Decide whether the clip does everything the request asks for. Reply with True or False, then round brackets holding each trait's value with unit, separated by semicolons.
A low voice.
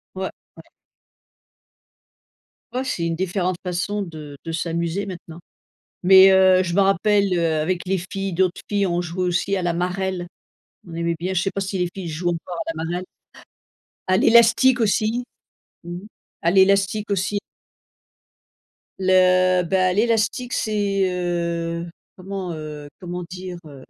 False (185 Hz)